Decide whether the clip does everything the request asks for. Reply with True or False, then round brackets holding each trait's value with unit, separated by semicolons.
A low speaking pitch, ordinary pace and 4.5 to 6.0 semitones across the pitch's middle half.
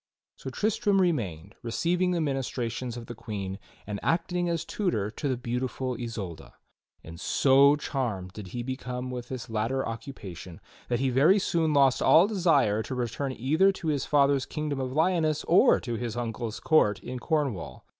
True (130 Hz; 165 wpm; 5.2 semitones)